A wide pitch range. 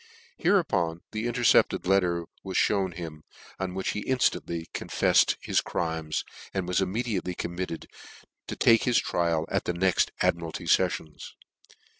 No: average, 2.7 semitones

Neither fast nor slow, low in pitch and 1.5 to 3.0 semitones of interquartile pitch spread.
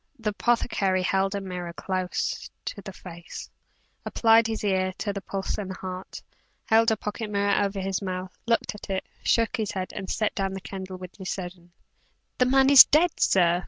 No: average, 185 wpm; high, 195 Hz; narrow, 2.5 semitones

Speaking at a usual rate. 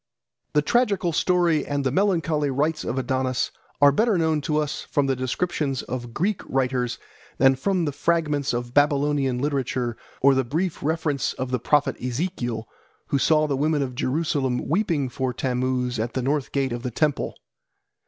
Yes: average, 170 wpm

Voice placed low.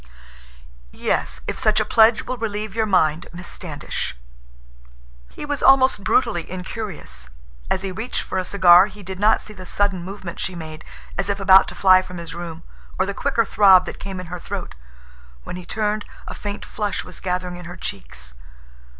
No: high, 190 Hz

